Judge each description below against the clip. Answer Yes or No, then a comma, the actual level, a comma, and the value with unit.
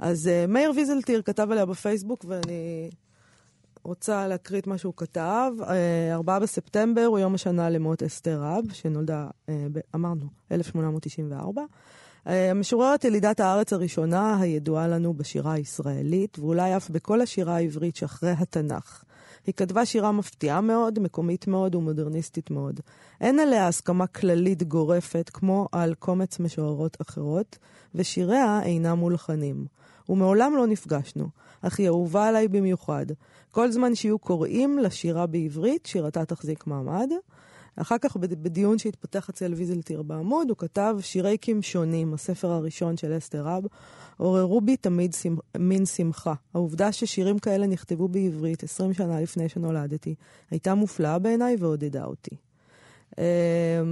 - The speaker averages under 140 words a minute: Yes, average, 125 wpm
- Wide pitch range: No, average, 3.7 semitones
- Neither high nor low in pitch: Yes, medium, 180 Hz